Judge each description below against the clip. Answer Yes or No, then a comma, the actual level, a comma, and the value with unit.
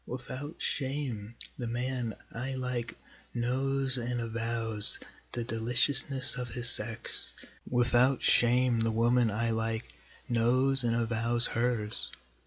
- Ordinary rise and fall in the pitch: No, narrow, 1.8 semitones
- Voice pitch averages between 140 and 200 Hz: No, low, 120 Hz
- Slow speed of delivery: Yes, slow, 115 wpm